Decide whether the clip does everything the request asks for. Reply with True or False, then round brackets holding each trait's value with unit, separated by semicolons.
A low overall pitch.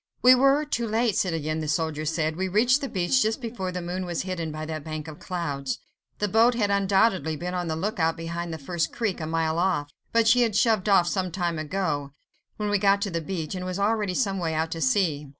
False (180 Hz)